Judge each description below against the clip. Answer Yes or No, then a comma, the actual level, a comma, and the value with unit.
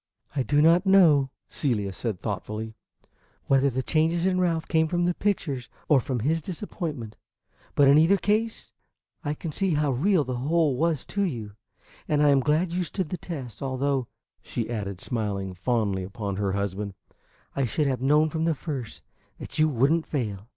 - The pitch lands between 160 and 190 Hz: No, medium, 140 Hz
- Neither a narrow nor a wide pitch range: No, wide, 5.9 semitones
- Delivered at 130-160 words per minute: No, average, 180 wpm